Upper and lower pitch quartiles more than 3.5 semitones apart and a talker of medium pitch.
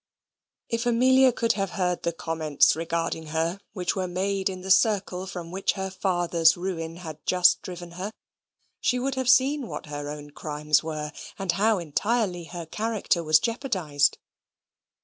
Yes: average, 4.2 semitones; medium, 180 Hz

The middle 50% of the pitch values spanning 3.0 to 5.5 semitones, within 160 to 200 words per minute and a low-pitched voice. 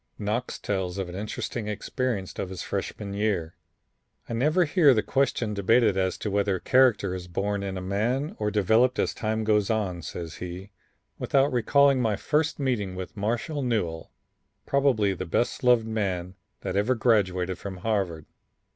Yes: average, 4.5 semitones; average, 165 wpm; low, 105 Hz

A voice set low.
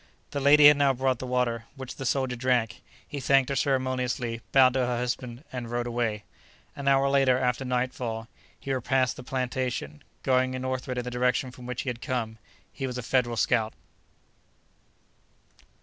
Yes: low, 125 Hz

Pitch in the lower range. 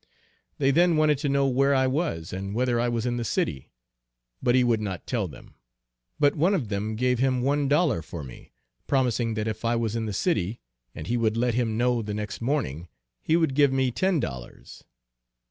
Yes: low, 120 Hz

